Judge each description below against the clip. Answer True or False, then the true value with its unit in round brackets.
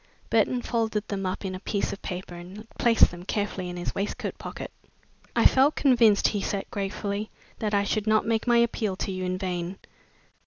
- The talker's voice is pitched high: True (200 Hz)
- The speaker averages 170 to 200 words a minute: True (195 wpm)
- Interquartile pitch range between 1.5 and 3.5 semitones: True (3.0 semitones)